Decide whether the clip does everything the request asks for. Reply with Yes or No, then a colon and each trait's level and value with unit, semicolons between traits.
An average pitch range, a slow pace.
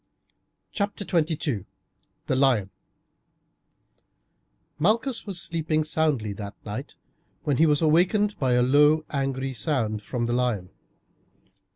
Yes: average, 4.9 semitones; slow, 110 wpm